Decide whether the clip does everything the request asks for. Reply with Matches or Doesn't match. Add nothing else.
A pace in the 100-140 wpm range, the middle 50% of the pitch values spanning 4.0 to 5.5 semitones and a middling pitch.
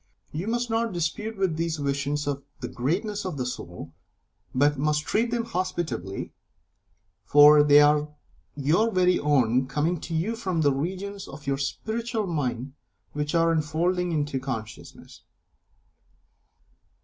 Matches